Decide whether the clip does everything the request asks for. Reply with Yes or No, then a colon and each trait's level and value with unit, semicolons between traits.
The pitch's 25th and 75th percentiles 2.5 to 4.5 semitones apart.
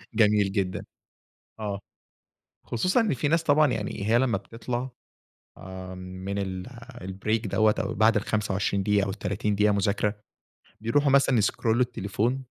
Yes: average, 3.2 semitones